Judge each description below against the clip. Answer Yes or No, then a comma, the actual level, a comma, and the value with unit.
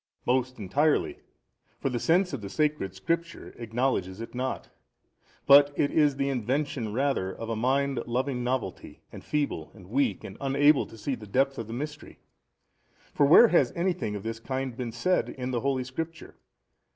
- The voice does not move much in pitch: No, average, 3.9 semitones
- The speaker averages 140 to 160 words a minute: No, average, 175 wpm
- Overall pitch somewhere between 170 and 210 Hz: No, low, 130 Hz